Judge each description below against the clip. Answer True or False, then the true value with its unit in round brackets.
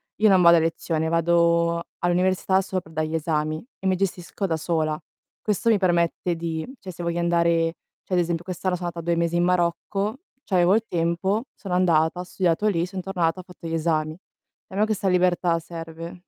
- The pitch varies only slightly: True (2.0 semitones)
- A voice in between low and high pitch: True (170 Hz)